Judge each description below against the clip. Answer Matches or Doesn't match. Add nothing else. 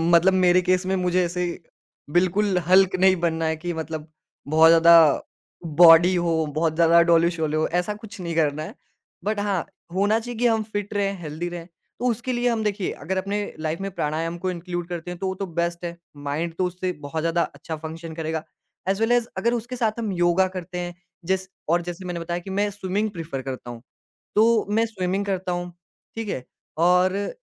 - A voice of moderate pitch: Matches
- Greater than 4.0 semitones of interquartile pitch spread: Doesn't match